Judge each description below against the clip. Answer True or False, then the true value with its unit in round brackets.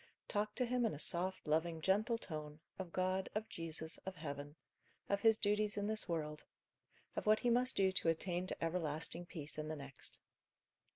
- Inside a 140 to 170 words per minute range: False (185 wpm)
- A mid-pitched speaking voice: True (180 Hz)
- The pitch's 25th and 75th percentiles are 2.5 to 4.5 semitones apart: False (4.9 semitones)